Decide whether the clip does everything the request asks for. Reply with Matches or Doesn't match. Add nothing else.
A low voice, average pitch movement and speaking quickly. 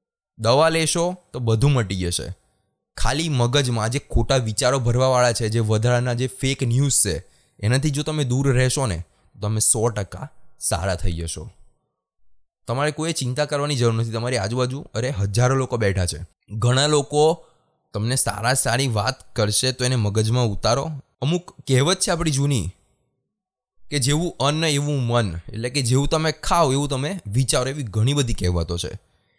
Matches